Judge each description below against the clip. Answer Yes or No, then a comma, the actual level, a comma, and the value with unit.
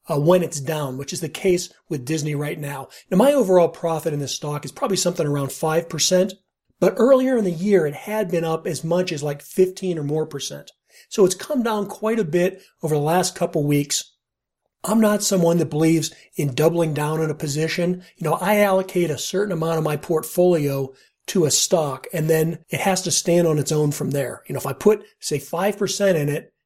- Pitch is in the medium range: Yes, medium, 165 Hz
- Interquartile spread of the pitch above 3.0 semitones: Yes, average, 3.6 semitones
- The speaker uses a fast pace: Yes, fast, 220 wpm